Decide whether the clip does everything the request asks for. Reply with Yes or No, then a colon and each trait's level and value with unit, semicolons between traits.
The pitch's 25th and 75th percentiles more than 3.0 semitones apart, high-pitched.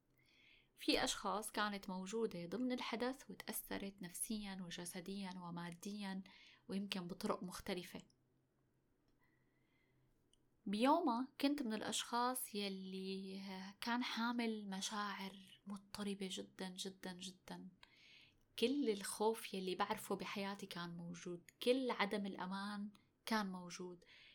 No: average, 2.7 semitones; high, 200 Hz